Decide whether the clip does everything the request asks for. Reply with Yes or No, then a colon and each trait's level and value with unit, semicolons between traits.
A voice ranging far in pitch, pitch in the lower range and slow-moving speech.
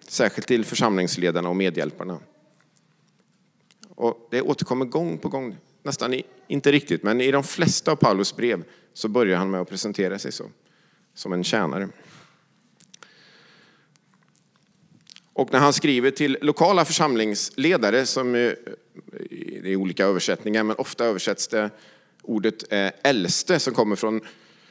Yes: wide, 6.7 semitones; low, 120 Hz; slow, 130 wpm